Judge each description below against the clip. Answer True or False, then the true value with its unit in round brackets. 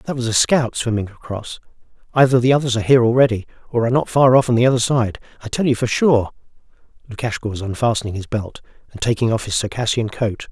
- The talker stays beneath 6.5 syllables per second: False (6.6 syllables/s)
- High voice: False (120 Hz)